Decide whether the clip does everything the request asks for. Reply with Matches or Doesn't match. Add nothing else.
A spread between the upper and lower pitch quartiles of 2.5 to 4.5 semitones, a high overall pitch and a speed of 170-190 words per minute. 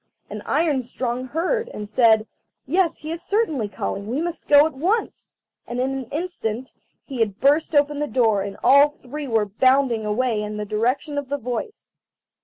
Doesn't match